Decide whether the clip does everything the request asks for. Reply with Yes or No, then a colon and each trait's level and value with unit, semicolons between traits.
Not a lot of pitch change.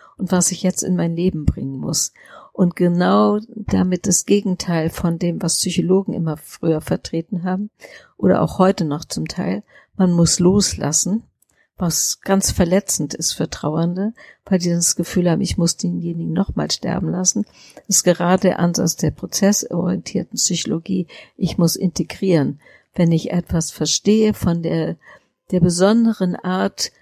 Yes: narrow, 2.3 semitones